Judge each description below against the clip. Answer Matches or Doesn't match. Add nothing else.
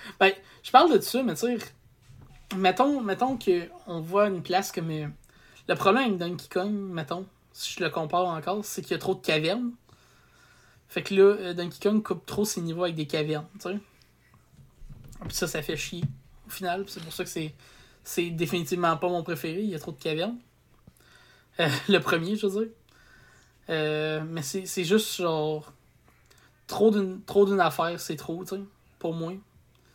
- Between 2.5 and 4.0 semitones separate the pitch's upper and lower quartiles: Matches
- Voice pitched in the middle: Matches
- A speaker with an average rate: Matches